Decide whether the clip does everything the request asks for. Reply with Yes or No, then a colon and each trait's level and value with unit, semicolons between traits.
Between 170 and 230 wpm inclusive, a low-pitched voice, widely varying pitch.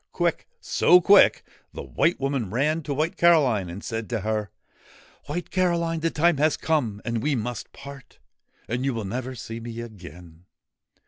Yes: average, 175 wpm; low, 125 Hz; wide, 6.1 semitones